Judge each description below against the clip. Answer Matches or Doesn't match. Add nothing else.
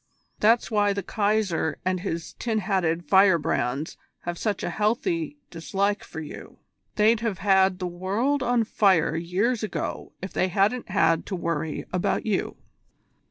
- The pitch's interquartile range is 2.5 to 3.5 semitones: Doesn't match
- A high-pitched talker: Matches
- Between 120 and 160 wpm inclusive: Matches